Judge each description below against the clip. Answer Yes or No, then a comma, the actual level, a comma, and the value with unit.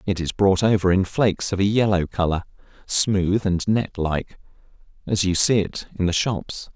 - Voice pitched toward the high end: No, very low, 95 Hz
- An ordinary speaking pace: Yes, average, 185 wpm